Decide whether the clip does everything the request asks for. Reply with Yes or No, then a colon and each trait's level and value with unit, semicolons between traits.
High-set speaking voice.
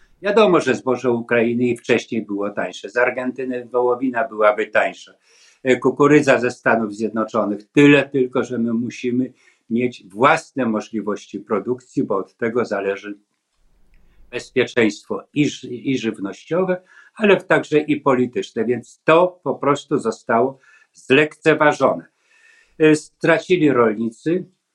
No: low, 125 Hz